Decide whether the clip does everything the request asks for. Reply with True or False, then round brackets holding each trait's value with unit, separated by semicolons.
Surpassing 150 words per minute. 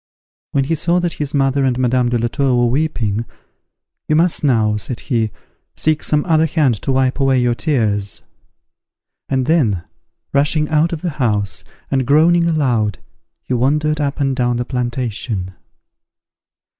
True (160 wpm)